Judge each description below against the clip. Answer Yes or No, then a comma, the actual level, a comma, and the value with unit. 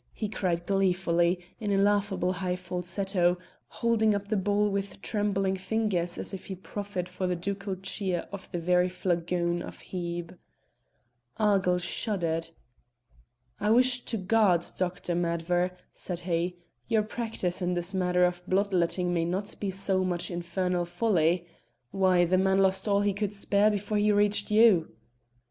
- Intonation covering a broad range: No, narrow, 2.4 semitones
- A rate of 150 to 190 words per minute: Yes, average, 155 wpm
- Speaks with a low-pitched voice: No, medium, 185 Hz